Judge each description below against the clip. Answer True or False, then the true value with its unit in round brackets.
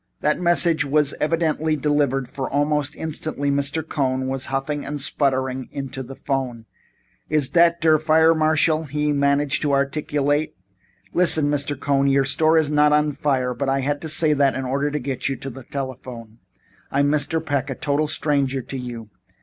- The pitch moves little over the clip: True (2.1 semitones)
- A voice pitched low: False (145 Hz)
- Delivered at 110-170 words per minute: False (180 wpm)